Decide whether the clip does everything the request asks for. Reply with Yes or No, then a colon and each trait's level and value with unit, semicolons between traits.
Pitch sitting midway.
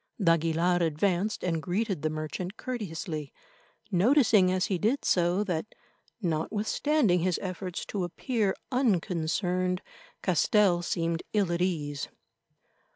Yes: medium, 180 Hz